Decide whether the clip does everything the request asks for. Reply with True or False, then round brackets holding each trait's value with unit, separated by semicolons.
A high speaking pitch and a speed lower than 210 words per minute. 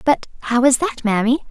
True (255 Hz; 200 wpm)